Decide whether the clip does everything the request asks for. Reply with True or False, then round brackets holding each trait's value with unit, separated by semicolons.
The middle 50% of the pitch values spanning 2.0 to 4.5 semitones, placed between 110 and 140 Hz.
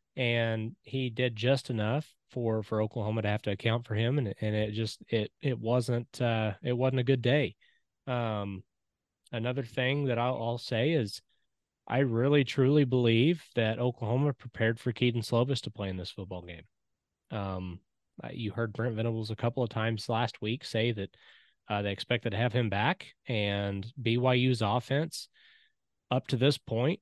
True (2.7 semitones; 120 Hz)